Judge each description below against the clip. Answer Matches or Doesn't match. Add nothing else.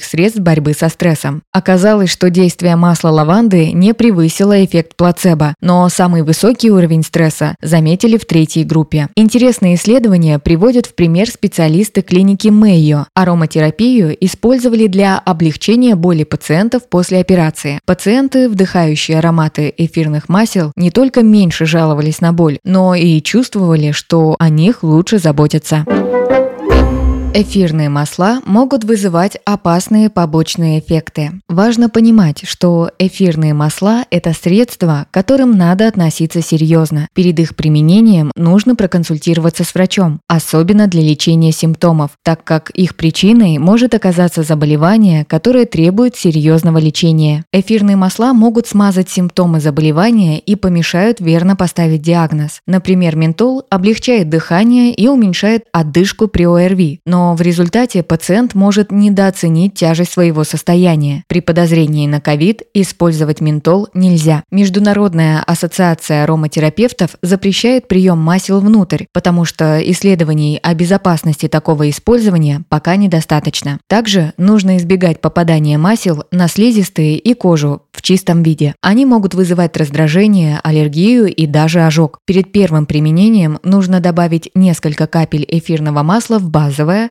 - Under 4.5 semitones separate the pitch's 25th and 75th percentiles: Matches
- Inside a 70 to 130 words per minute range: Matches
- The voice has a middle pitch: Matches